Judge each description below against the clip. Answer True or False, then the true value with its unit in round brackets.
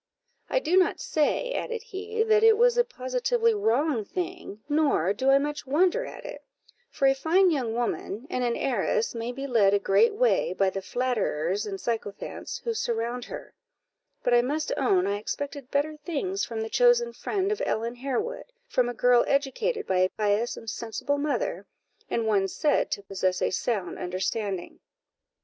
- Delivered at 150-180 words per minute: True (175 wpm)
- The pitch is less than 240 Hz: False (265 Hz)